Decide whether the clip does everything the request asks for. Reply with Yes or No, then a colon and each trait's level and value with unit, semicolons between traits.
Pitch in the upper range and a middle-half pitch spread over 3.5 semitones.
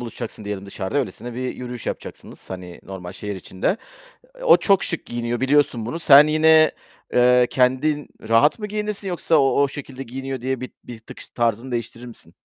No: low, 125 Hz; average, 4.2 semitones